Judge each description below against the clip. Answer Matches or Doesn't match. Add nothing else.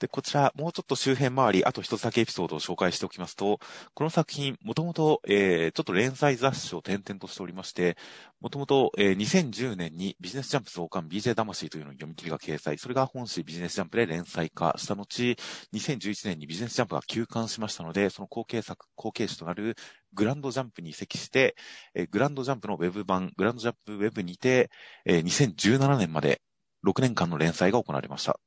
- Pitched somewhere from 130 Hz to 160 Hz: Doesn't match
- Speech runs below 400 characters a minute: Doesn't match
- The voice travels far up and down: Matches